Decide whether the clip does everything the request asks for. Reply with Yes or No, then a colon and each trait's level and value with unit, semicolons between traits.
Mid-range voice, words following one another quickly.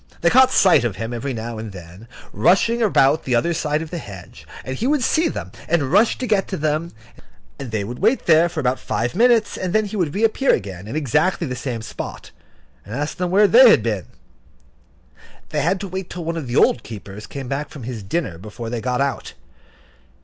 Yes: medium, 150 Hz; fast, 220 wpm